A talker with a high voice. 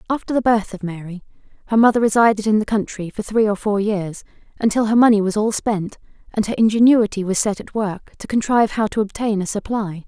Yes: high, 210 Hz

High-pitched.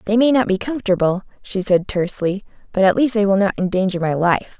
Yes: high, 200 Hz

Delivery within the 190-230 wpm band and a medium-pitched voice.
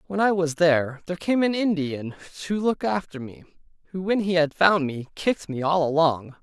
Yes: fast, 205 wpm; medium, 170 Hz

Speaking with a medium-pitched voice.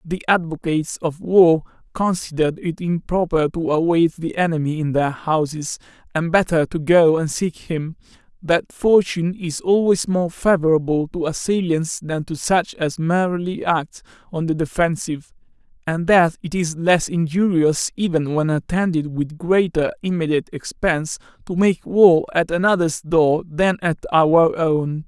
Yes: medium, 165 Hz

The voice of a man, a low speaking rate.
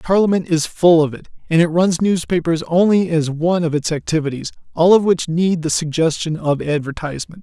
No: male; average, 180 wpm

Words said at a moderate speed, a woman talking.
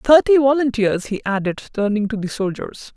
Yes: average, 160 wpm; female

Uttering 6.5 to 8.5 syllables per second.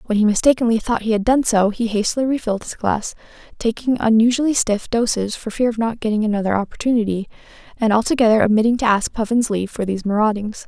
Yes: 6.6 syllables/s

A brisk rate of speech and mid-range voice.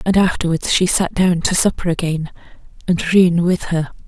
No: average, 175 wpm; medium, 175 Hz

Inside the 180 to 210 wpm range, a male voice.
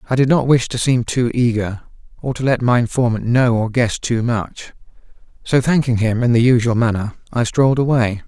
Yes: fast, 205 wpm; male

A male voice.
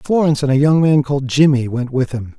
Yes: male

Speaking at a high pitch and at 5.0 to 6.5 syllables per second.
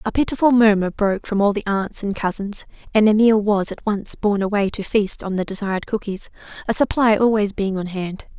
Yes: high, 205 Hz; 5.6 syllables/s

